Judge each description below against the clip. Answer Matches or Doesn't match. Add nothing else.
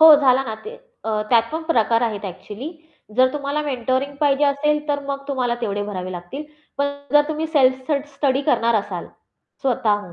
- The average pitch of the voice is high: Matches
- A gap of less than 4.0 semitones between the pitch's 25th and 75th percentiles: Doesn't match